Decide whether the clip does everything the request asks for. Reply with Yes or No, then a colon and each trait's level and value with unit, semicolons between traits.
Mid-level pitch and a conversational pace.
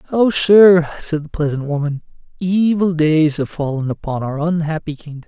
Yes: medium, 160 Hz; average, 160 wpm